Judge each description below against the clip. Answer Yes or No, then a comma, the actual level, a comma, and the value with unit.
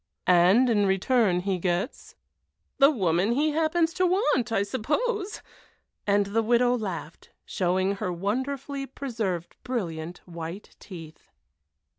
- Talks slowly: Yes, slow, 120 wpm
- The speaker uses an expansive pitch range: Yes, wide, 6.8 semitones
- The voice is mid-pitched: No, high, 210 Hz